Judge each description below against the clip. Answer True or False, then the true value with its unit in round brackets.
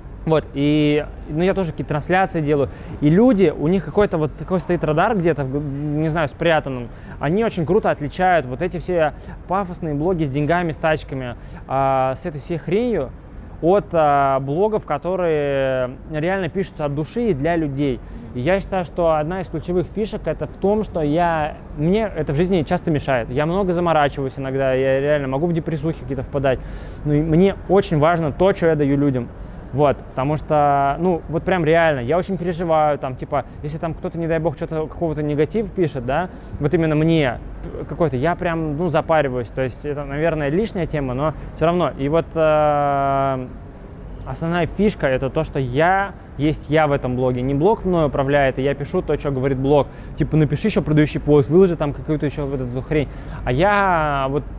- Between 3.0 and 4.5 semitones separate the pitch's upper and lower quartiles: True (3.6 semitones)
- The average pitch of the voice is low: False (155 Hz)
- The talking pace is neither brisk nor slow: False (185 wpm)